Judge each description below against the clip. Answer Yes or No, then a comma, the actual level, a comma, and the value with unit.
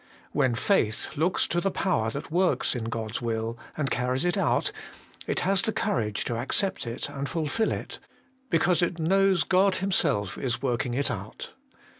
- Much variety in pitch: Yes, wide, 7.7 semitones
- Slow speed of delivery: No, average, 170 wpm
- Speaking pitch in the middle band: Yes, medium, 145 Hz